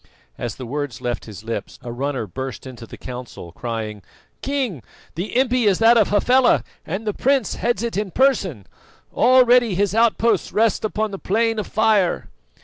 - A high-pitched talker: Yes, high, 200 Hz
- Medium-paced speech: Yes, average, 170 wpm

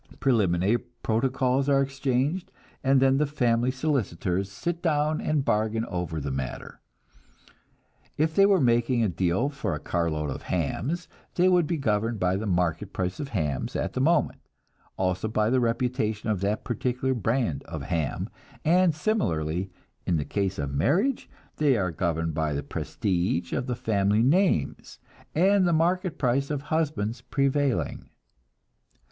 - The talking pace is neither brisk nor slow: Yes, average, 155 wpm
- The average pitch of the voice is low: Yes, low, 120 Hz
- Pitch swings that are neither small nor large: No, wide, 7.7 semitones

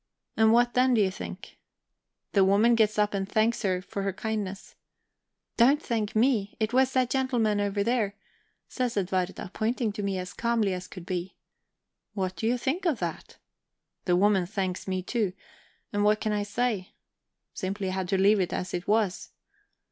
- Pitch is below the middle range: No, high, 205 Hz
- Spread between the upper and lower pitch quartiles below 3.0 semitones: No, average, 3.6 semitones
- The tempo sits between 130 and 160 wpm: No, average, 175 wpm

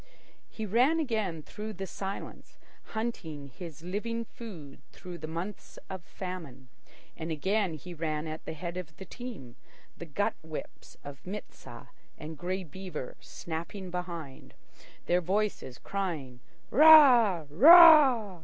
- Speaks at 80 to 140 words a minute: Yes, slow, 135 wpm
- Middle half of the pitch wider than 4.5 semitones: Yes, average, 5.1 semitones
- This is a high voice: No, medium, 180 Hz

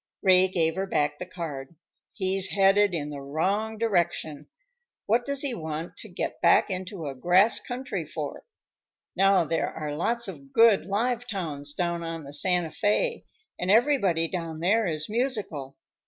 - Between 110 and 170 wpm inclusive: Yes, average, 160 wpm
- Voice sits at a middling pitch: Yes, medium, 180 Hz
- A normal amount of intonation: Yes, average, 4.9 semitones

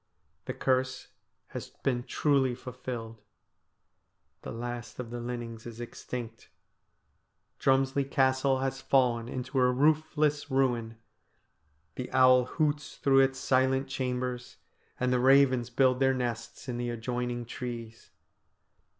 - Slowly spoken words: Yes, slow, 120 wpm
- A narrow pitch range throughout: Yes, narrow, 1.7 semitones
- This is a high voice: No, low, 125 Hz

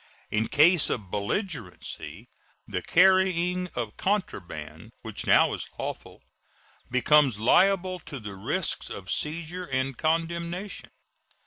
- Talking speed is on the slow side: Yes, slow, 110 wpm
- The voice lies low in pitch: No, medium, 155 Hz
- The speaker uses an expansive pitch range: Yes, wide, 8.3 semitones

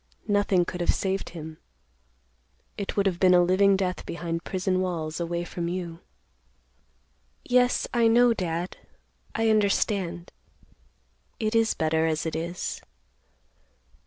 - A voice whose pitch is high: No, medium, 180 Hz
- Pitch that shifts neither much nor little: Yes, average, 3.0 semitones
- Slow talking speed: Yes, slow, 130 wpm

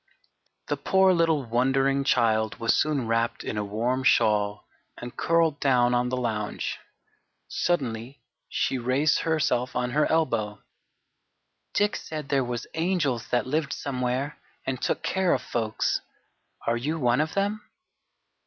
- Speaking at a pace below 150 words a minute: Yes, average, 140 wpm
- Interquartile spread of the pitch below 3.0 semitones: No, average, 4.5 semitones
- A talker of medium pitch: No, low, 130 Hz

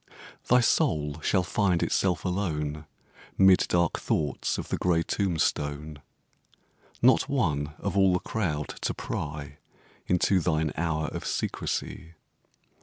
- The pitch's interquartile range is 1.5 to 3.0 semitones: No, average, 3.8 semitones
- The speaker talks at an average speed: No, slow, 120 wpm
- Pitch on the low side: Yes, very low, 80 Hz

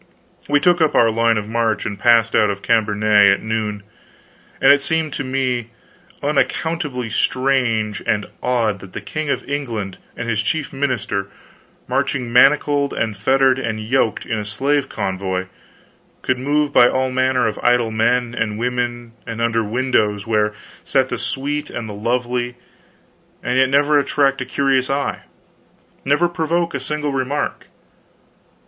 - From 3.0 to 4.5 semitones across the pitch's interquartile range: Yes, average, 3.9 semitones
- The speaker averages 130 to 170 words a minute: Yes, average, 155 wpm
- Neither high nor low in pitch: No, low, 125 Hz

